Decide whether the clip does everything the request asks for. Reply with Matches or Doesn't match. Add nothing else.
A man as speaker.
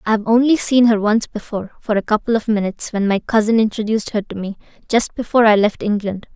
Doesn't match